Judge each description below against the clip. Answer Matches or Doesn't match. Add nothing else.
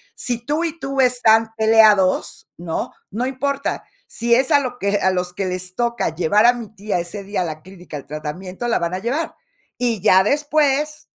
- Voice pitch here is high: Matches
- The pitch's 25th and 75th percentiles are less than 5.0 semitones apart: Doesn't match